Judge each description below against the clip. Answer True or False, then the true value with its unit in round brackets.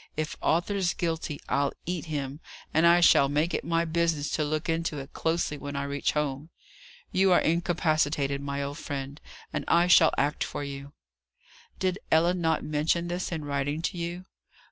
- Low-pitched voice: False (155 Hz)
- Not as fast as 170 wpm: False (175 wpm)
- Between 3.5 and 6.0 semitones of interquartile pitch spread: False (3.0 semitones)